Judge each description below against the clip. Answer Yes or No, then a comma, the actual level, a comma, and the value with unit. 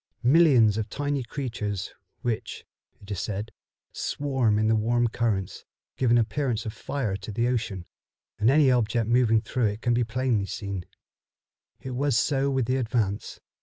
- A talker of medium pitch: No, low, 115 Hz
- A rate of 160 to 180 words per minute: Yes, average, 165 wpm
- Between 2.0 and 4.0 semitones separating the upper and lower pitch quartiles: Yes, average, 3.3 semitones